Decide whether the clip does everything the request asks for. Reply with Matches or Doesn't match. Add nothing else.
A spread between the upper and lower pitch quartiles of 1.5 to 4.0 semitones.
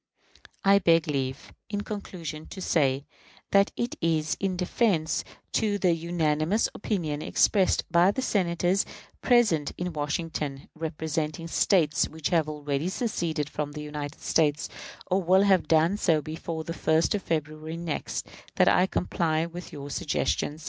Matches